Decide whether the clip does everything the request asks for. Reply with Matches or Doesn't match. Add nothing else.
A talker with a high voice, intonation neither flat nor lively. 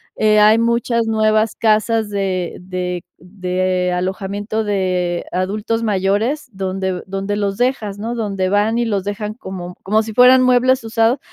Matches